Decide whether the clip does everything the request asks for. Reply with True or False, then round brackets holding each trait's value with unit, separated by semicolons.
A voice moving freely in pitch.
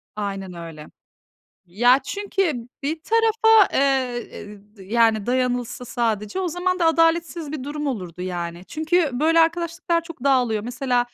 True (7.6 semitones)